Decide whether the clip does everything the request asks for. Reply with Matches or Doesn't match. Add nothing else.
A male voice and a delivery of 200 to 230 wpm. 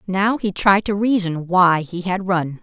Doesn't match